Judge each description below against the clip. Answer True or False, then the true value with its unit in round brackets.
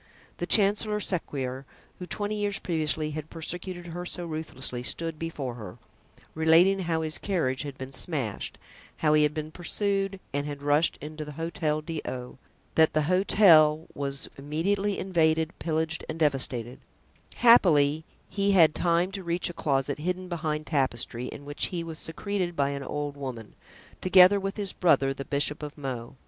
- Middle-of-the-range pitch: True (160 Hz)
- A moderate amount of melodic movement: True (3.9 semitones)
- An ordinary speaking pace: True (160 wpm)